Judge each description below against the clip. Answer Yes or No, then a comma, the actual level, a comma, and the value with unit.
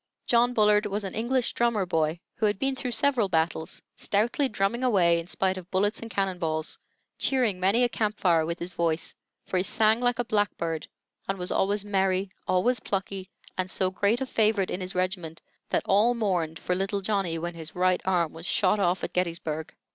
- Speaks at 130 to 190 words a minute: No, average, 200 wpm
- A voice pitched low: No, high, 195 Hz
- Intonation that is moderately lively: Yes, average, 3.6 semitones